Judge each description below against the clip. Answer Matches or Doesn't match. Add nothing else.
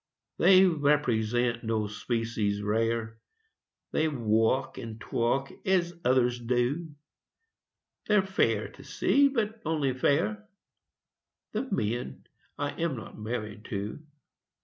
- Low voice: Matches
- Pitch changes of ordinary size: Doesn't match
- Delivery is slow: Matches